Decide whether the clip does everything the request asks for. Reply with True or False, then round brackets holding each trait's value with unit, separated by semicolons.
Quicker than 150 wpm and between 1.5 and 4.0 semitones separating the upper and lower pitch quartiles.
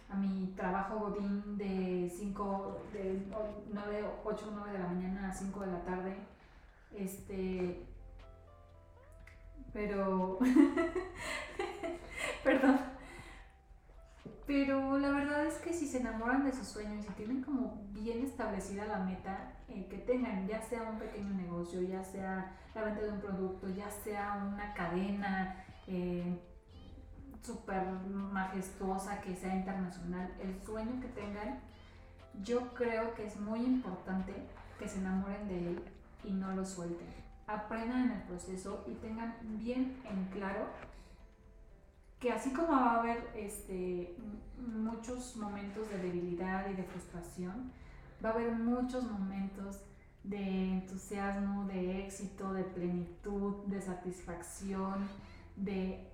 False (130 wpm; 2.9 semitones)